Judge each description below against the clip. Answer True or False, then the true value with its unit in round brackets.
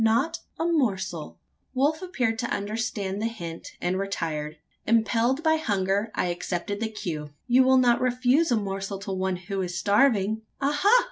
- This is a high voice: True (215 Hz)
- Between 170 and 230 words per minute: False (160 wpm)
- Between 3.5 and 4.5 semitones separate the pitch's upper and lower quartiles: False (5.1 semitones)